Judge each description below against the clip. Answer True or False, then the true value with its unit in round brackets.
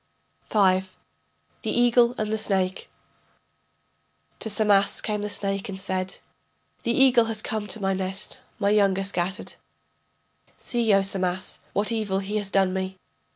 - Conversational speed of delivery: True (150 wpm)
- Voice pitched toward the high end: True (200 Hz)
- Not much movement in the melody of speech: True (2.2 semitones)